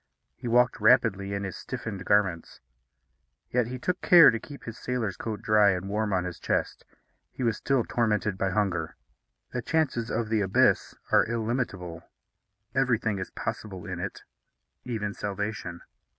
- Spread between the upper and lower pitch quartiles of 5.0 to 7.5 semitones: No, average, 3.6 semitones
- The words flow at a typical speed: Yes, average, 155 wpm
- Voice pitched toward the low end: Yes, low, 110 Hz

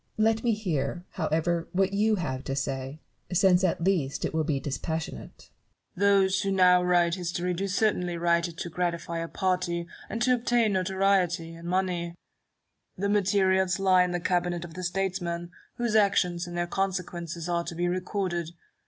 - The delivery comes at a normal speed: Yes, average, 175 wpm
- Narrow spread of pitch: Yes, narrow, 2.2 semitones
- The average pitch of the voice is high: No, medium, 180 Hz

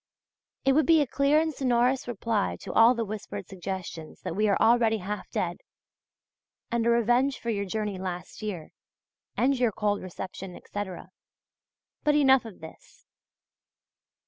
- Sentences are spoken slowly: No, average, 150 wpm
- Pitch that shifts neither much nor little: Yes, average, 4.5 semitones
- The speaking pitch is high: Yes, high, 225 Hz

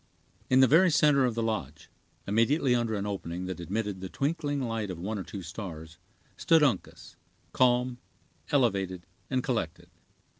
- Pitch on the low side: Yes, low, 110 Hz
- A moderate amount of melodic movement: No, wide, 5.8 semitones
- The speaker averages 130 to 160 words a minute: Yes, average, 155 wpm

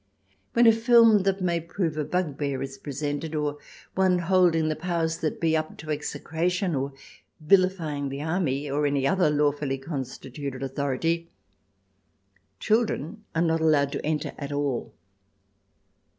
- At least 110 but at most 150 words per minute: Yes, average, 145 wpm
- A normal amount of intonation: Yes, average, 3.8 semitones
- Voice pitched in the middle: Yes, medium, 155 Hz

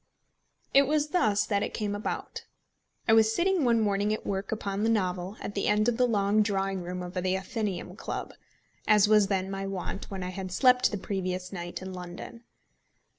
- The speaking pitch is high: Yes, high, 200 Hz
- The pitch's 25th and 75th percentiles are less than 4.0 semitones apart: Yes, average, 2.7 semitones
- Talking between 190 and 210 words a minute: Yes, average, 195 wpm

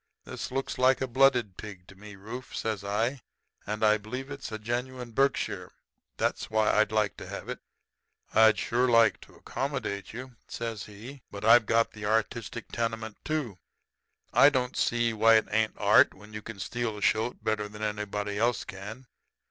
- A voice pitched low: Yes, low, 110 Hz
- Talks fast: No, average, 175 wpm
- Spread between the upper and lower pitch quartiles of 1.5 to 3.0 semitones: Yes, average, 2.7 semitones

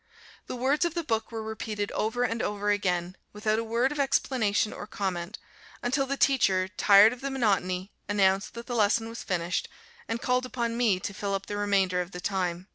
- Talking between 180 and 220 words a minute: Yes, average, 200 wpm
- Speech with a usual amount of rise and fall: Yes, average, 3.9 semitones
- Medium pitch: No, high, 210 Hz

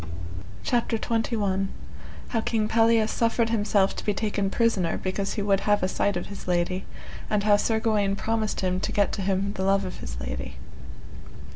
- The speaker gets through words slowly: No, average, 180 wpm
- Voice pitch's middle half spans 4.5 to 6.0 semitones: No, narrow, 2.6 semitones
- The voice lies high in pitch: Yes, high, 205 Hz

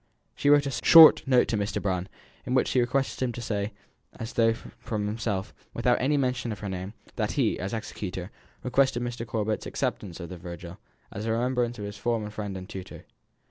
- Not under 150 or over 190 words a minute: No, fast, 205 wpm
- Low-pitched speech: Yes, low, 110 Hz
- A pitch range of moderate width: Yes, average, 3.6 semitones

